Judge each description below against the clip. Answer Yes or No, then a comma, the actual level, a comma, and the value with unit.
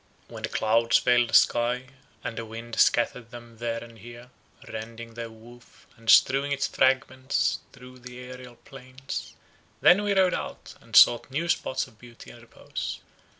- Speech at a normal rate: Yes, average, 160 wpm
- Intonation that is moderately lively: No, narrow, 2.1 semitones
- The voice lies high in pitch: No, low, 120 Hz